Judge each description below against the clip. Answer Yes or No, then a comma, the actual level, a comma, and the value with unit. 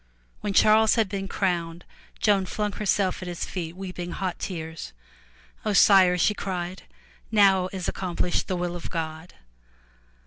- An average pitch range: No, narrow, 2.2 semitones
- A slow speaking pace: No, average, 145 wpm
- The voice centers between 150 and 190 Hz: Yes, medium, 185 Hz